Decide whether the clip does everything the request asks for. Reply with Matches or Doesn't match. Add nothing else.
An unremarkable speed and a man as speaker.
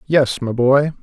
Matches